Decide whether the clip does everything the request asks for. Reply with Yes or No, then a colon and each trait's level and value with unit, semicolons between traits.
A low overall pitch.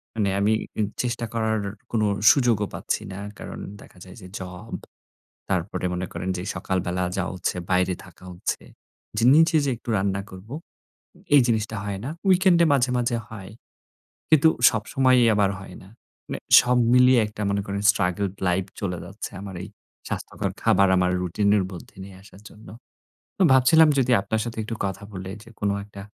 Yes: low, 105 Hz